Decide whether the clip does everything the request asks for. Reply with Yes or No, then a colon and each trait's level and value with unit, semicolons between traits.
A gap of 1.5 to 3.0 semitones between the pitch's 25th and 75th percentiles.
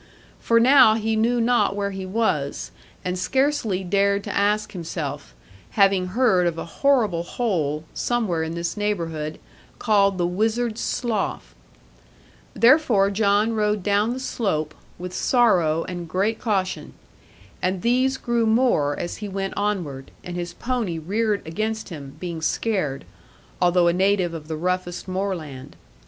No: average, 4.3 semitones